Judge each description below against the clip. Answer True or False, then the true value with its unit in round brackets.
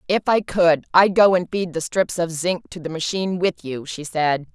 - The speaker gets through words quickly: True (240 wpm)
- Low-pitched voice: False (175 Hz)